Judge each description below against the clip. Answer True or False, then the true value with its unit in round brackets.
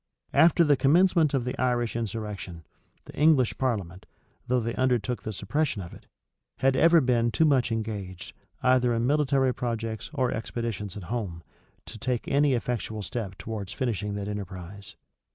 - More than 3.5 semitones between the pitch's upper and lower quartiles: True (4.2 semitones)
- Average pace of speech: True (155 wpm)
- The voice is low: True (115 Hz)